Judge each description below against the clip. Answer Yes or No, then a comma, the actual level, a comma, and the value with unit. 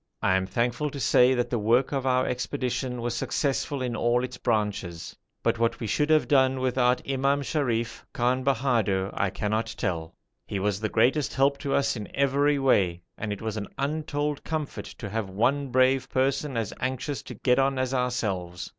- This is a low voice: Yes, low, 125 Hz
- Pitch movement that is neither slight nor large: Yes, average, 3.8 semitones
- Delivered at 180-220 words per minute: Yes, average, 190 wpm